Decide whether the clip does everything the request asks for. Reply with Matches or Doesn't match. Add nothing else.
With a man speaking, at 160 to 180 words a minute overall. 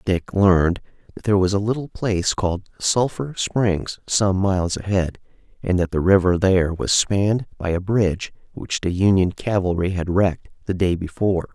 Matches